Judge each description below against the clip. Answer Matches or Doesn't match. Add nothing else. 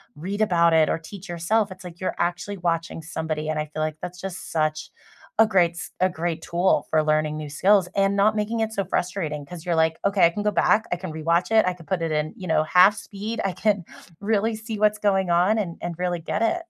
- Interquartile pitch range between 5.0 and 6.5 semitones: Doesn't match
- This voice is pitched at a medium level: Matches